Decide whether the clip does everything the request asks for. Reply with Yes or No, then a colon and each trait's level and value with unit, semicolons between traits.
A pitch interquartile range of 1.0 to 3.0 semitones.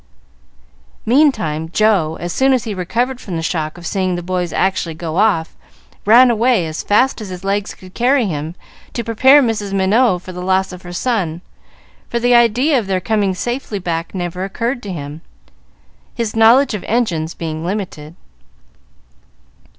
No: average, 5.1 semitones